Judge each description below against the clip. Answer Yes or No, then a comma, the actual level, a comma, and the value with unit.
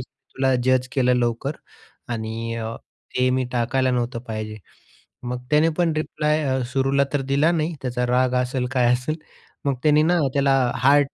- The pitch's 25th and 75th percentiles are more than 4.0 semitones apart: No, average, 2.7 semitones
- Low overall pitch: Yes, low, 130 Hz